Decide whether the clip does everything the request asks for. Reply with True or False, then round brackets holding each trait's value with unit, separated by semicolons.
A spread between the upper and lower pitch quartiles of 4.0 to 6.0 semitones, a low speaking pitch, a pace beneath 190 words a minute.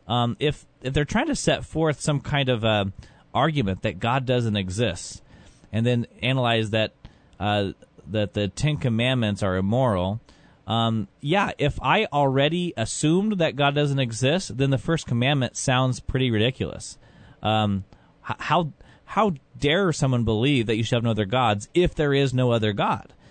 True (4.8 semitones; 125 Hz; 165 wpm)